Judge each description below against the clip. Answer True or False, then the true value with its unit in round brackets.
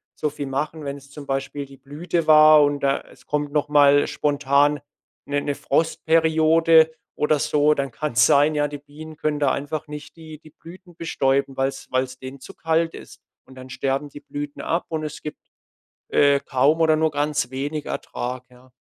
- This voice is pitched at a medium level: True (145 Hz)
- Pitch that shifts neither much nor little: False (2.0 semitones)